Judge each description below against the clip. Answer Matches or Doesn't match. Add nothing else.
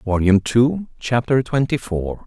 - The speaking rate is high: Doesn't match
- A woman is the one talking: Doesn't match